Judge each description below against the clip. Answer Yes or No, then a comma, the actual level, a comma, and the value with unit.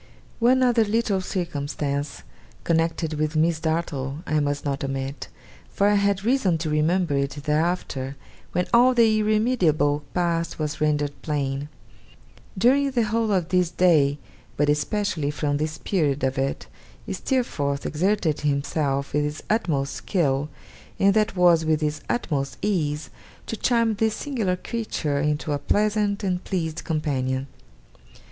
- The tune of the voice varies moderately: No, wide, 5.7 semitones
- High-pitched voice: No, medium, 160 Hz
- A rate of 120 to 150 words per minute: Yes, average, 140 wpm